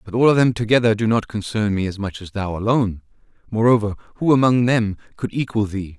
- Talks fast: Yes, fast, 210 wpm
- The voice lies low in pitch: Yes, low, 110 Hz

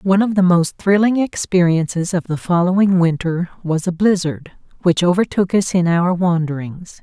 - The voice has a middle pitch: Yes, medium, 180 Hz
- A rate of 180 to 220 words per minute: No, average, 160 wpm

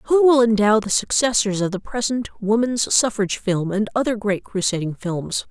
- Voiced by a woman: Yes, female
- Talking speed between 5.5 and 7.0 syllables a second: No, 4.8 syllables/s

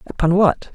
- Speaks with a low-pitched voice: No, medium, 180 Hz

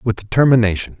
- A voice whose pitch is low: Yes, low, 115 Hz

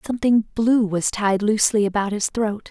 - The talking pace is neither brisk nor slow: Yes, average, 175 wpm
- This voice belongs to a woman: Yes, female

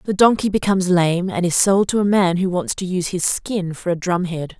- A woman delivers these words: Yes, female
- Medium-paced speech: No, fast, 250 wpm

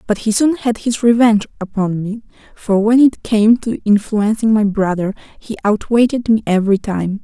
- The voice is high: Yes, high, 215 Hz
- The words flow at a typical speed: Yes, average, 175 wpm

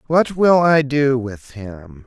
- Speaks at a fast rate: No, average, 175 wpm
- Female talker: No, male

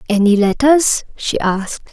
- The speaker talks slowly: Yes, slow, 125 wpm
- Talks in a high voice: Yes, high, 225 Hz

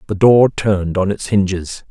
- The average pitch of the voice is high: No, low, 100 Hz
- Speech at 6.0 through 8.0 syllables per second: No, 4.7 syllables/s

